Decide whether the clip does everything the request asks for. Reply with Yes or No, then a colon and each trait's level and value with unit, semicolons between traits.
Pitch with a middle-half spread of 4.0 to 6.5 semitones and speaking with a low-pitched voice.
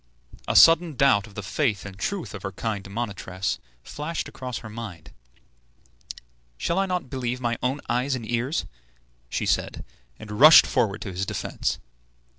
Yes: wide, 5.5 semitones; low, 120 Hz